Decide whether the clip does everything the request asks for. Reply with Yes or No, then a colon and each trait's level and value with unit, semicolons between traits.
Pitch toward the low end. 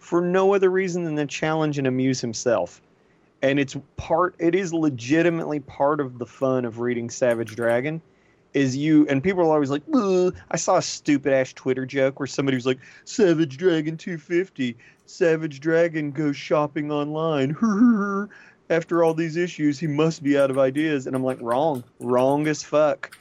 No: medium, 150 Hz